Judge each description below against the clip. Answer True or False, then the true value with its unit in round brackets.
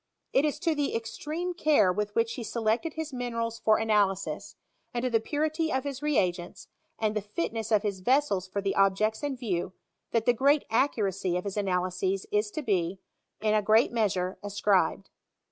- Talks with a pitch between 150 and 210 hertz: False (220 Hz)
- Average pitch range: True (4.7 semitones)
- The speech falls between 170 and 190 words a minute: True (185 wpm)